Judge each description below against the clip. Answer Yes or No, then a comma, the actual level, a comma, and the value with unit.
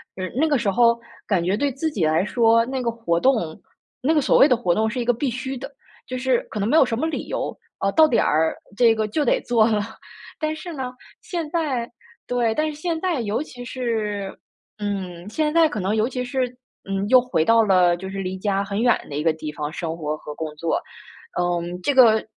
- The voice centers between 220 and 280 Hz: Yes, high, 230 Hz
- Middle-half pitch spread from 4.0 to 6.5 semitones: Yes, average, 5.3 semitones